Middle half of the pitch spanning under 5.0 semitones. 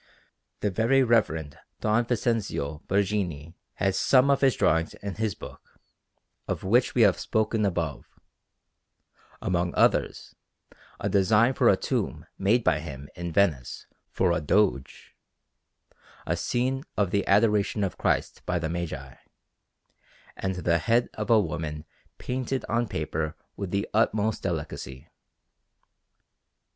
No: average, 5.3 semitones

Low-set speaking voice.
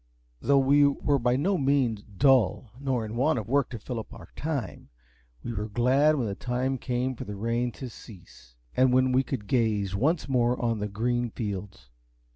Yes: low, 125 Hz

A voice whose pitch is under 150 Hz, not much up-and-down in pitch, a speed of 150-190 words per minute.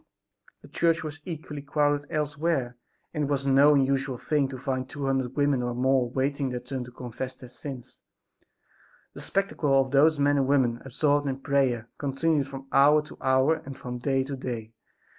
Yes: low, 135 Hz; narrow, 1.9 semitones; average, 180 wpm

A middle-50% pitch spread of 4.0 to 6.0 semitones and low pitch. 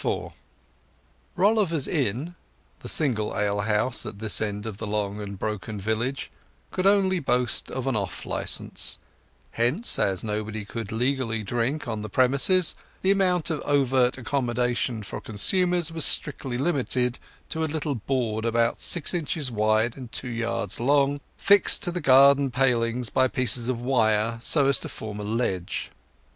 Yes: average, 4.6 semitones; low, 125 Hz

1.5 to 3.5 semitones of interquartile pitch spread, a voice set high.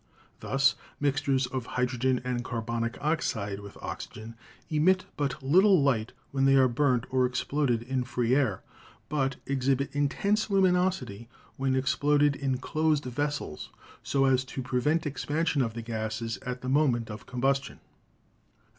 No: average, 3.1 semitones; low, 135 Hz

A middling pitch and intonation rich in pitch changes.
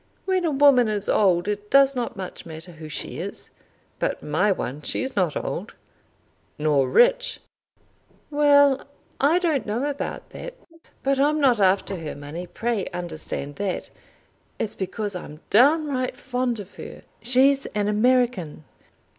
No: high, 215 Hz; wide, 7.4 semitones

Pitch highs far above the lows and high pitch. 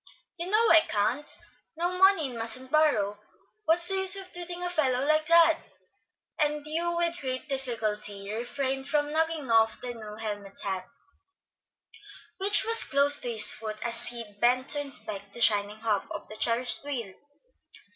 Yes: wide, 6.6 semitones; very high, 265 Hz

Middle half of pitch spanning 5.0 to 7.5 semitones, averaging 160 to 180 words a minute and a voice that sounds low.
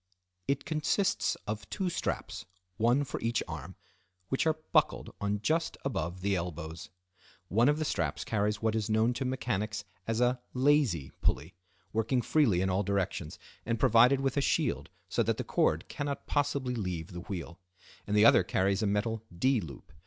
Yes: wide, 5.6 semitones; average, 170 wpm; low, 110 Hz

